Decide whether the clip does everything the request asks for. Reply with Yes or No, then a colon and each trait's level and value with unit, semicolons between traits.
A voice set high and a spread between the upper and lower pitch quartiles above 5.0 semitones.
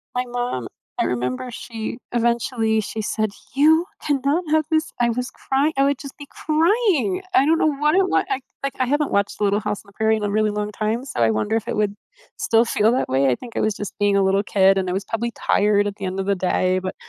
Yes: high, 225 Hz; wide, 5.5 semitones